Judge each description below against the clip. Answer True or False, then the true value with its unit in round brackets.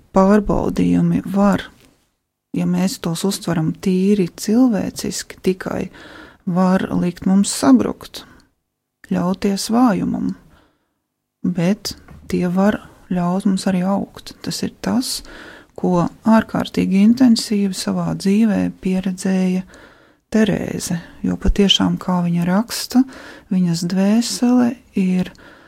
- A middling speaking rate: False (100 wpm)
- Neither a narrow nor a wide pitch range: True (3.3 semitones)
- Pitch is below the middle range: False (195 Hz)